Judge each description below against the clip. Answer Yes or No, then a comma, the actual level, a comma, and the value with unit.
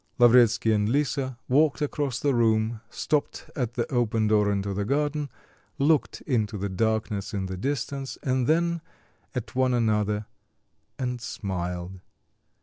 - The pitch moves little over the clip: No, average, 4.6 semitones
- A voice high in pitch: No, low, 120 Hz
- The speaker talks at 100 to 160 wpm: Yes, average, 140 wpm